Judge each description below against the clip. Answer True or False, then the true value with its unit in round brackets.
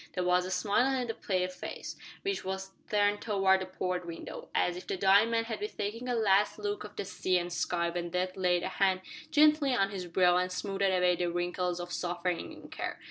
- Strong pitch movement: False (2.6 semitones)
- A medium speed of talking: False (225 wpm)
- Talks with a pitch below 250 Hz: True (190 Hz)